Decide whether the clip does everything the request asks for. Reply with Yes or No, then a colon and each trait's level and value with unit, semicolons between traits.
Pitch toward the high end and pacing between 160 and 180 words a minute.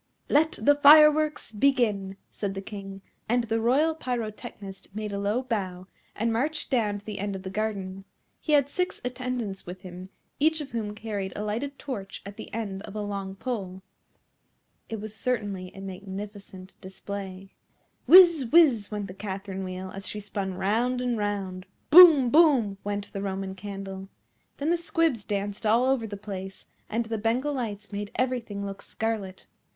Yes: high, 210 Hz; average, 170 wpm